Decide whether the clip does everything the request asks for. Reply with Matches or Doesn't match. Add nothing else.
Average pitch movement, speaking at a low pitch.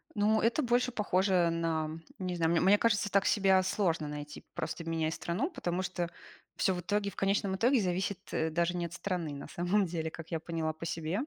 Doesn't match